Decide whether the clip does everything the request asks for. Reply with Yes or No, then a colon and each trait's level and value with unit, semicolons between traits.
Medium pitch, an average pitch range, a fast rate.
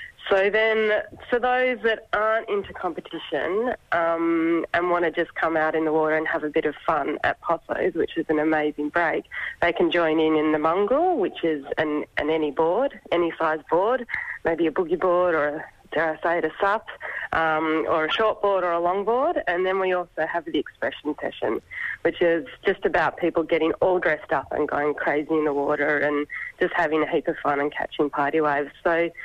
Yes: medium, 165 Hz; average, 3.8 semitones; fast, 210 wpm